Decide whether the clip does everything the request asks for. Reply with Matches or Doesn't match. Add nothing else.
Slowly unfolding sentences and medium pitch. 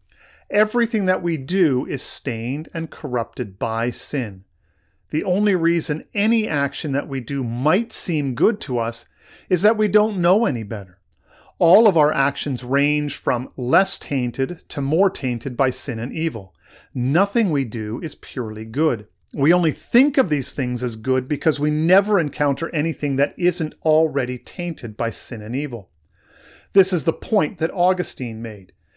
Doesn't match